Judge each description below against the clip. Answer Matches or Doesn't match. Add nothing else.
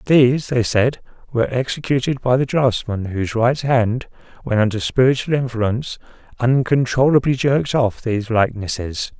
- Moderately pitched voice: Doesn't match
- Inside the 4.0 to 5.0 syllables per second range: Doesn't match